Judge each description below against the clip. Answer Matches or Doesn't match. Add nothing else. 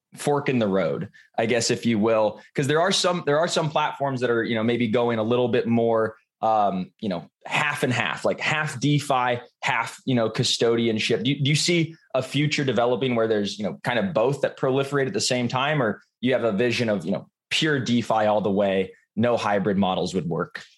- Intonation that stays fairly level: Doesn't match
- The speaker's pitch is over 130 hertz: Doesn't match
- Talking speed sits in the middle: Doesn't match